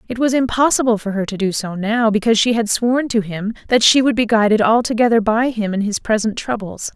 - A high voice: Yes, high, 225 Hz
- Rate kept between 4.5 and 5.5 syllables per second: No, 5.8 syllables/s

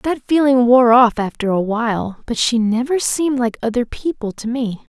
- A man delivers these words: No, female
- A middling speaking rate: Yes, average, 190 wpm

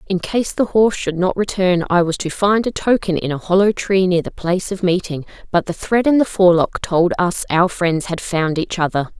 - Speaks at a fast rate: Yes, fast, 235 wpm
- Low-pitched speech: No, medium, 185 Hz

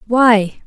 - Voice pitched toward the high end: Yes, high, 225 Hz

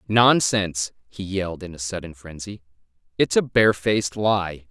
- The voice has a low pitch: Yes, very low, 95 Hz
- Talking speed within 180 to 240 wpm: No, average, 140 wpm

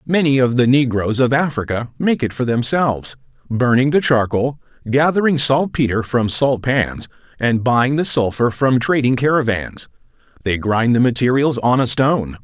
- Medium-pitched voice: No, low, 125 Hz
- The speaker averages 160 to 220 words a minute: No, average, 150 wpm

